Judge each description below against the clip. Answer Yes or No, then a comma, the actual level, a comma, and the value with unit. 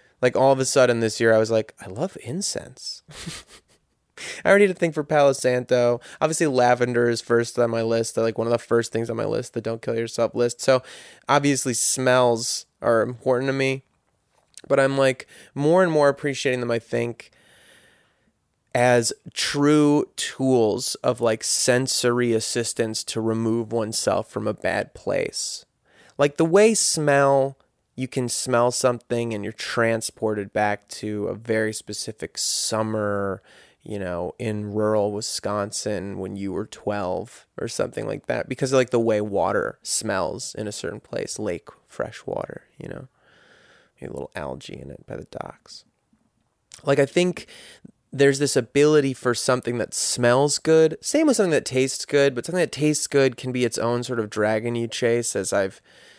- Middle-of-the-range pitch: No, low, 120 Hz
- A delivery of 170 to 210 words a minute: Yes, average, 175 wpm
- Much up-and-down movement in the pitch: No, average, 3.4 semitones